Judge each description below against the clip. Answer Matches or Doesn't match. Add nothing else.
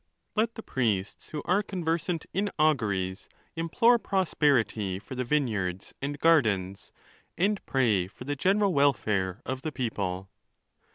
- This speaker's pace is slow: Matches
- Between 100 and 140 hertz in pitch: Matches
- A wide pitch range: Matches